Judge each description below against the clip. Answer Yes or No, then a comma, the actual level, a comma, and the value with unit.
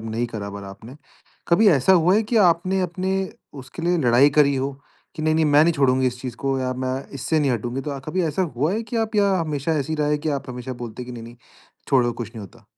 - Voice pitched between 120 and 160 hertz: Yes, medium, 140 Hz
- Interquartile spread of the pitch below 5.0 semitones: No, average, 5.3 semitones